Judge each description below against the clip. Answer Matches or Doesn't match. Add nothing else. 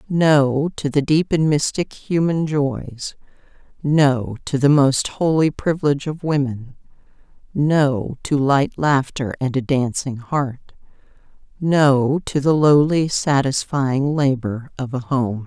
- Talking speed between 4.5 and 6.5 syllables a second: Doesn't match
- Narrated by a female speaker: Matches